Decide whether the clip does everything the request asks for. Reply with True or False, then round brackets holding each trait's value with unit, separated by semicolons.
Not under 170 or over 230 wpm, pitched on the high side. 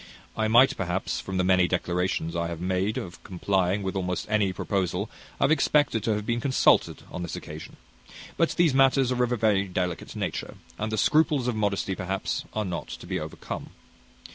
False (190 wpm; 100 Hz)